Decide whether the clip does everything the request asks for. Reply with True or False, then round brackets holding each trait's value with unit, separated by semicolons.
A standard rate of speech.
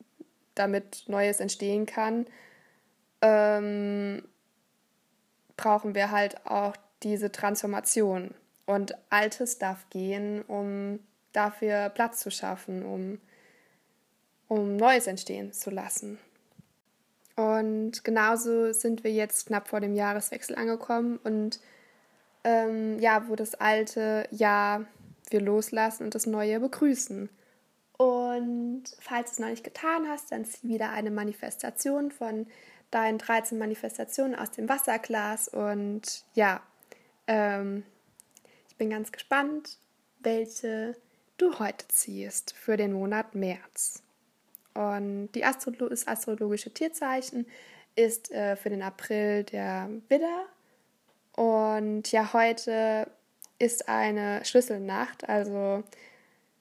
False (110 wpm)